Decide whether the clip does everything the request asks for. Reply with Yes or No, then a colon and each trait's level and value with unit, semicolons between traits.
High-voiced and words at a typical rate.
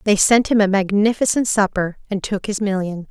Yes: high, 200 Hz; average, 195 wpm